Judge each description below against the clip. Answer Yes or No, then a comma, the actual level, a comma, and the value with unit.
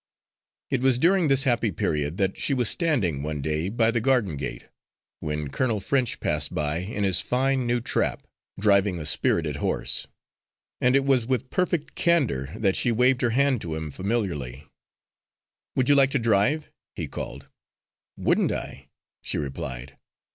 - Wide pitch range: Yes, wide, 9.0 semitones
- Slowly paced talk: No, average, 160 wpm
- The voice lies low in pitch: Yes, low, 110 Hz